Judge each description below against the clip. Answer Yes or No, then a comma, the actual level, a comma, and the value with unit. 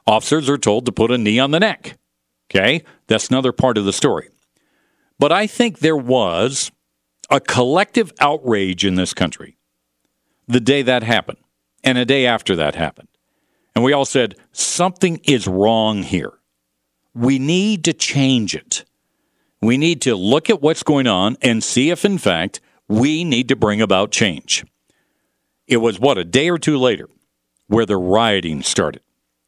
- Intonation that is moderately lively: No, wide, 7.3 semitones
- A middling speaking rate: Yes, average, 165 wpm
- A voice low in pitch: Yes, low, 120 Hz